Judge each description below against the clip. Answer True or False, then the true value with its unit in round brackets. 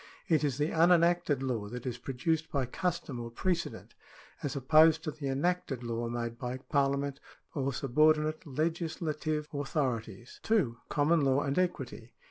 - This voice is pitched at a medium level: True (145 Hz)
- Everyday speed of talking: True (150 wpm)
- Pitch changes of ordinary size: True (4.0 semitones)